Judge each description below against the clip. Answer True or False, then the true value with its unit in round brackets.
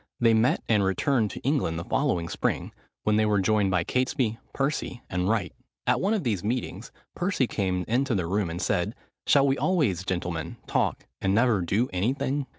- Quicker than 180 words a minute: True (190 wpm)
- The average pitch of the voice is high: False (110 Hz)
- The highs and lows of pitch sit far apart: True (5.8 semitones)